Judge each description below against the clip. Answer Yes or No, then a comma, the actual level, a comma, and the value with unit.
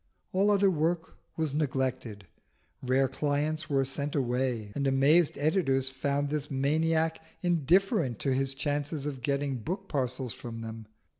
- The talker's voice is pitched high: No, medium, 140 Hz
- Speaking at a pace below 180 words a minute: Yes, average, 140 wpm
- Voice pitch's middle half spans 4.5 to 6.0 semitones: No, average, 3.2 semitones